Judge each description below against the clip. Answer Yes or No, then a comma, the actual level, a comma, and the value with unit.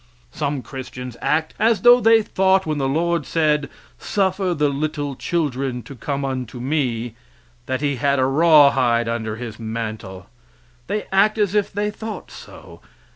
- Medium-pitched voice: Yes, medium, 145 Hz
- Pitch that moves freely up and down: Yes, wide, 5.9 semitones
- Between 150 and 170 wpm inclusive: Yes, average, 155 wpm